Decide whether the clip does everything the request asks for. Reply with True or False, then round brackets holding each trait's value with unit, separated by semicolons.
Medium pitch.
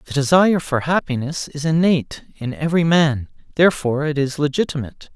True (145 Hz)